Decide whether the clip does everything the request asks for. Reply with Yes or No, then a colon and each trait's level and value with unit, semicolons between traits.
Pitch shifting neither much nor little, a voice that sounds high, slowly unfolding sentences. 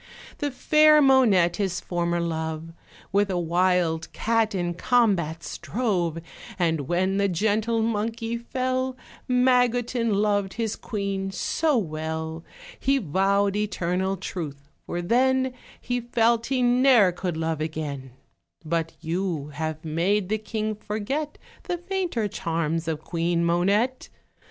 No: wide, 5.7 semitones; high, 195 Hz; slow, 125 wpm